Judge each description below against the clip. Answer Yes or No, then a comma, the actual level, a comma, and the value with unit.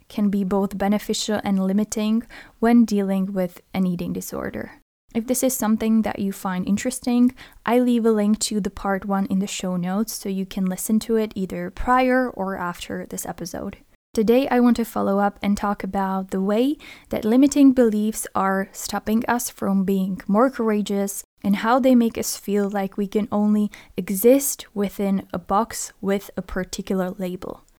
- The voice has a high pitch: Yes, high, 205 Hz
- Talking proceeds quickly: No, average, 180 wpm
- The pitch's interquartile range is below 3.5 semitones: Yes, average, 2.8 semitones